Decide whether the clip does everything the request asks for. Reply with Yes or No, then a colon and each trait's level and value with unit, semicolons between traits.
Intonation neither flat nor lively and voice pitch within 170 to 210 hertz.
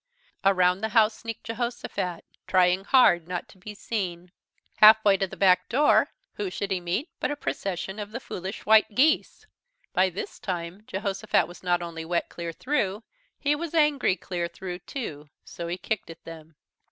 Yes: average, 3.8 semitones; high, 190 Hz